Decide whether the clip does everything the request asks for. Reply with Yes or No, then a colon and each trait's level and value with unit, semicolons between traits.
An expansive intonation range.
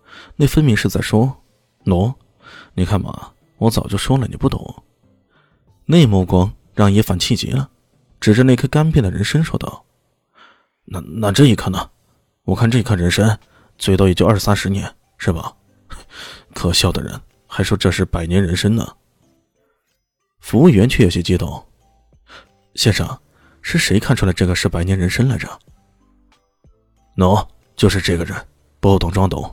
No: average, 4.4 semitones